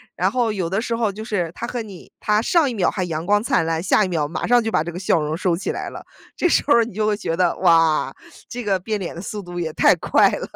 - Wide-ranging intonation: No, average, 4.5 semitones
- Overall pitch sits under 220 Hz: Yes, high, 195 Hz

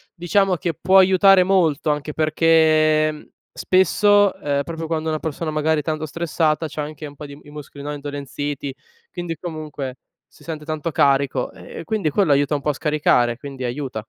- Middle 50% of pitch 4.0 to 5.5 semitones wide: No, narrow, 2.4 semitones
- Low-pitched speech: No, medium, 155 Hz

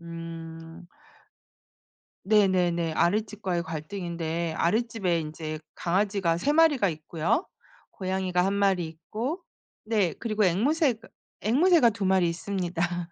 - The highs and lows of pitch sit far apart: No, average, 4.1 semitones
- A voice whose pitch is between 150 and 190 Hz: Yes, medium, 185 Hz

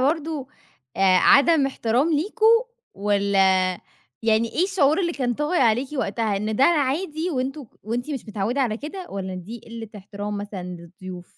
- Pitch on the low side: No, high, 235 Hz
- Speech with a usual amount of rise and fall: No, wide, 6.7 semitones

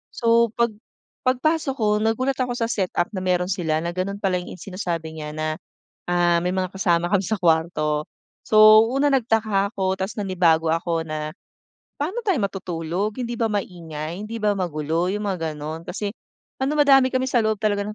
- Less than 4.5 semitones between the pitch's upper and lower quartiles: No, average, 4.9 semitones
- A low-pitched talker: No, high, 190 Hz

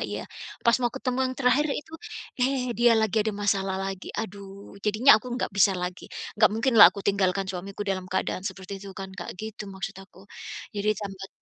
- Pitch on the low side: No, high, 200 Hz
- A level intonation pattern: No, average, 3.3 semitones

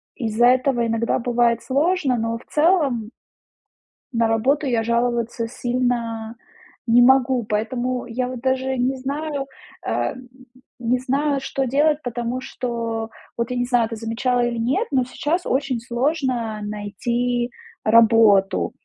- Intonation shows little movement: Yes, narrow, 2.3 semitones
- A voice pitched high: Yes, high, 245 Hz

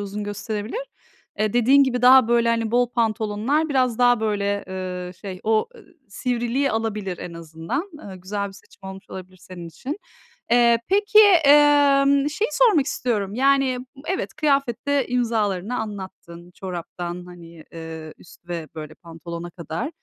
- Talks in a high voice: Yes, high, 215 Hz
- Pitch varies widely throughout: Yes, wide, 6.0 semitones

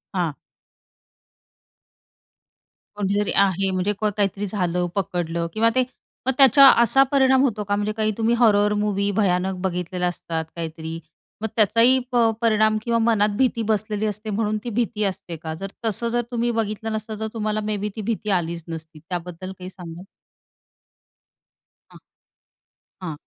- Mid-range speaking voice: No, high, 205 Hz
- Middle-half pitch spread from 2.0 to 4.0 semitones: Yes, average, 3.6 semitones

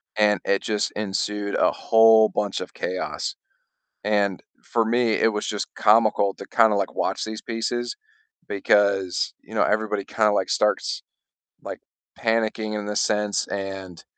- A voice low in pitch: Yes, low, 105 Hz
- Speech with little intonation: Yes, narrow, 1.6 semitones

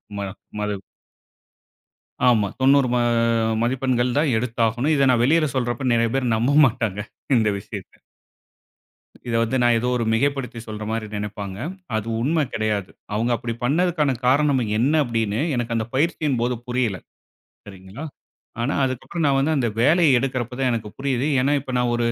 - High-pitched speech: No, low, 120 Hz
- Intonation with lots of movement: No, average, 3.2 semitones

